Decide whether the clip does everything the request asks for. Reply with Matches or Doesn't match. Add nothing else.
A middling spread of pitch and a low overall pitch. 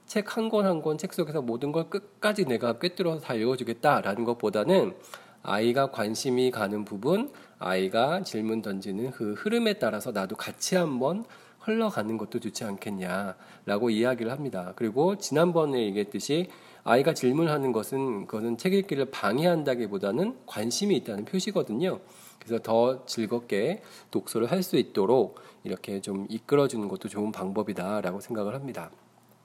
Doesn't match